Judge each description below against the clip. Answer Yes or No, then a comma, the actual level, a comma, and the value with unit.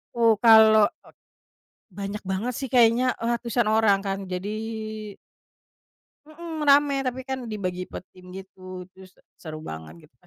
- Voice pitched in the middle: No, high, 215 Hz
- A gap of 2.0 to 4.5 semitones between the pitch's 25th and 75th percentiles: No, average, 5.0 semitones